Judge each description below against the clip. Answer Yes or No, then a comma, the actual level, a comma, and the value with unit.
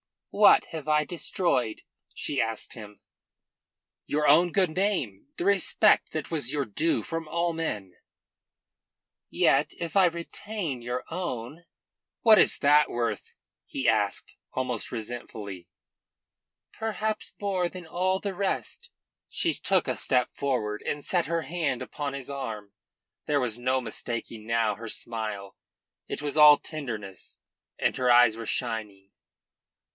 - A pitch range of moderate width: No, wide, 6.8 semitones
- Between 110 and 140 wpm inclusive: Yes, slow, 135 wpm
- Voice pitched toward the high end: No, medium, 140 Hz